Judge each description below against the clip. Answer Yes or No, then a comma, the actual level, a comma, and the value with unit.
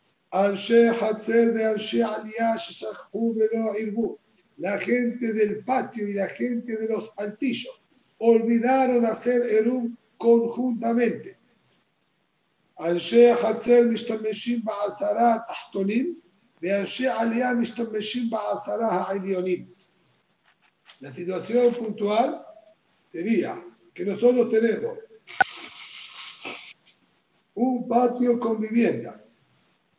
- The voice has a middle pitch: No, high, 230 Hz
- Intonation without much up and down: Yes, narrow, 2.0 semitones